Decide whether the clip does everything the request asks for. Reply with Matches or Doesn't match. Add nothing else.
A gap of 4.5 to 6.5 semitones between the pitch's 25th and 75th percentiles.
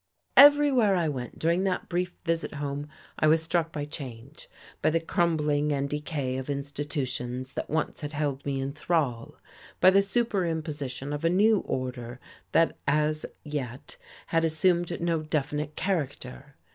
Doesn't match